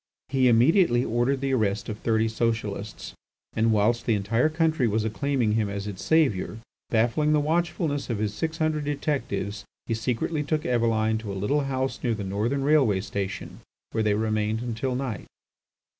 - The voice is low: Yes, low, 115 Hz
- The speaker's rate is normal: Yes, average, 170 wpm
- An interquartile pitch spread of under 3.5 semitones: No, average, 4.6 semitones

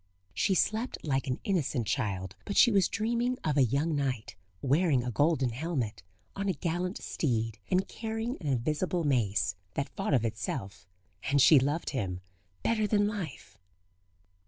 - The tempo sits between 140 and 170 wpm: Yes, average, 155 wpm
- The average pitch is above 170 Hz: No, medium, 145 Hz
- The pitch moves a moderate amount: No, wide, 7.9 semitones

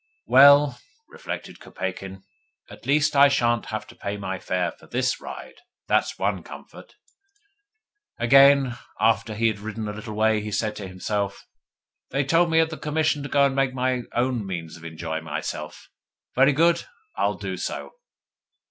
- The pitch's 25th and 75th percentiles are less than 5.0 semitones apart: No, average, 5.3 semitones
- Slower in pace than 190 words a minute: Yes, average, 165 wpm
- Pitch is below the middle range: Yes, low, 120 Hz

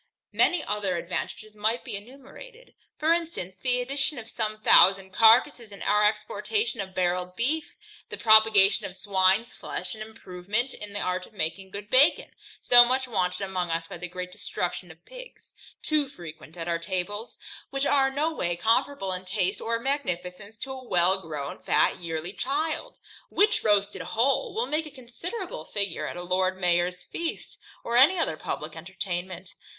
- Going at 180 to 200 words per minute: No, average, 170 wpm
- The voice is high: Yes, high, 210 Hz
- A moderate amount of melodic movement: No, wide, 6.4 semitones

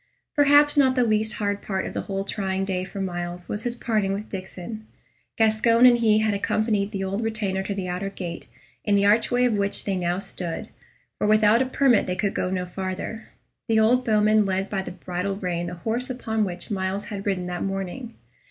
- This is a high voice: Yes, high, 200 Hz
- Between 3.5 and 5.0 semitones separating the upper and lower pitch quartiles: No, average, 2.7 semitones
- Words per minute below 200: No, fast, 205 wpm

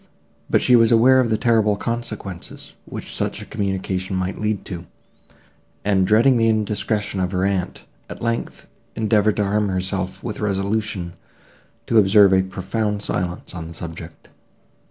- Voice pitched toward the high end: No, low, 100 Hz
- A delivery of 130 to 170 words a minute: Yes, average, 155 wpm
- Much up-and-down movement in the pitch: No, average, 2.8 semitones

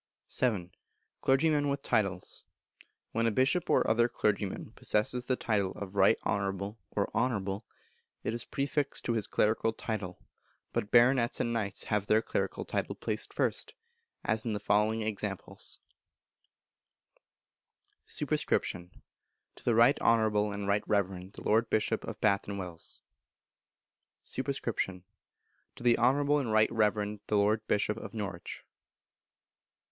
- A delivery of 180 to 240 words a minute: No, slow, 135 wpm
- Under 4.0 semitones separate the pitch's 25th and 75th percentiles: Yes, average, 2.8 semitones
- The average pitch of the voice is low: Yes, low, 110 Hz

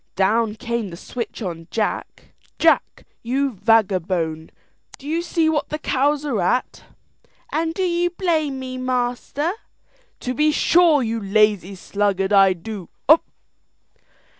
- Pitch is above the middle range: Yes, high, 240 Hz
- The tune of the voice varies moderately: No, wide, 7.1 semitones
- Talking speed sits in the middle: No, slow, 125 wpm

